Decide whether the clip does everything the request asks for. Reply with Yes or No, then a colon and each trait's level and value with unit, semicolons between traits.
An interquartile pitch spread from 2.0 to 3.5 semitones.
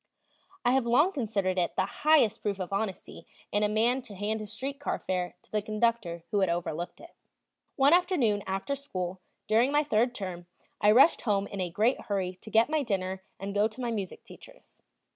No: average, 4.7 semitones